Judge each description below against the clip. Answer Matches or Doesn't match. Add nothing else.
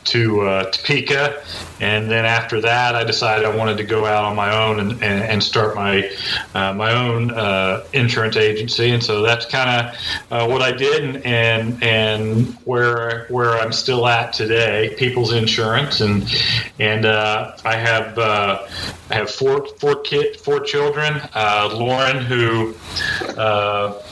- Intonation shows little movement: Matches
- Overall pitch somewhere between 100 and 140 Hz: Matches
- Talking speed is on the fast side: Doesn't match